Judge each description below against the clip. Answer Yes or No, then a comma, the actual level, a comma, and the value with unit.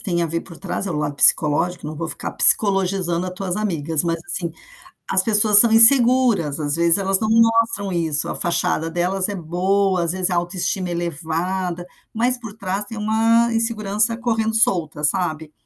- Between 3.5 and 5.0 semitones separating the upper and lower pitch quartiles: Yes, average, 4.3 semitones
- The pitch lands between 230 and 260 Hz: No, medium, 185 Hz